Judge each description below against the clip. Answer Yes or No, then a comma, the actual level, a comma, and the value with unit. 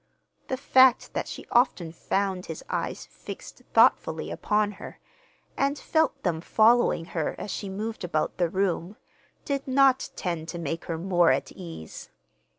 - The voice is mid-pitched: No, high, 195 Hz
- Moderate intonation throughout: No, wide, 6.3 semitones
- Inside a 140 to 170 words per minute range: Yes, average, 155 wpm